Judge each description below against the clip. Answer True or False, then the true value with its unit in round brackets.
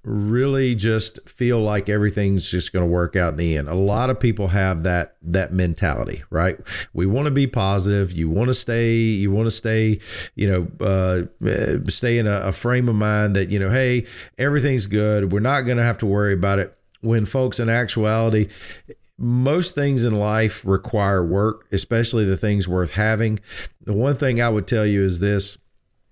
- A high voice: False (105 Hz)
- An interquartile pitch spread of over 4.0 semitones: False (3.3 semitones)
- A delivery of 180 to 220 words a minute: True (195 wpm)